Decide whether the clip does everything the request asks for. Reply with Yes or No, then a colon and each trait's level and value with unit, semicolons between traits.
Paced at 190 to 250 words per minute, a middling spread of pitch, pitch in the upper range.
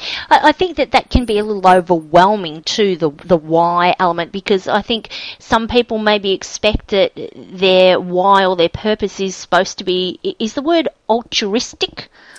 No: average, 170 wpm; average, 4.2 semitones; high, 195 Hz